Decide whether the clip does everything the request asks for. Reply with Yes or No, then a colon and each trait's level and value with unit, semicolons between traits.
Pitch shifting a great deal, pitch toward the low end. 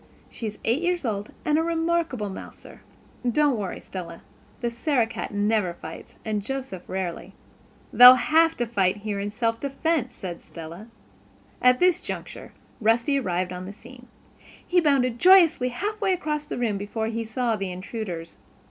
No: wide, 6.4 semitones; high, 235 Hz